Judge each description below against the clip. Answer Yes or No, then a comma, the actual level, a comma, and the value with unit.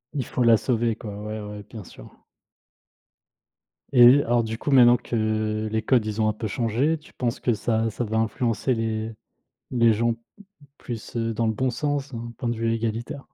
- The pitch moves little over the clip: Yes, narrow, 1.9 semitones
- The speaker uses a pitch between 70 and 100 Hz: No, low, 115 Hz